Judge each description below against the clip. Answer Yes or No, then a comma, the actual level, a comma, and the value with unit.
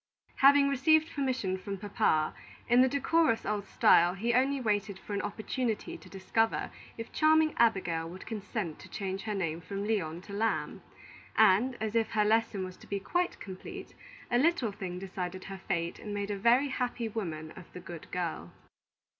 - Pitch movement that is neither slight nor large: Yes, average, 4.4 semitones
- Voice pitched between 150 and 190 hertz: No, high, 205 Hz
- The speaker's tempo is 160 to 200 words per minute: Yes, average, 180 wpm